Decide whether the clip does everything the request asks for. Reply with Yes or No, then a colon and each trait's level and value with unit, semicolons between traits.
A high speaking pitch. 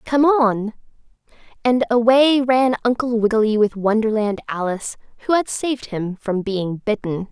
Yes: high, 230 Hz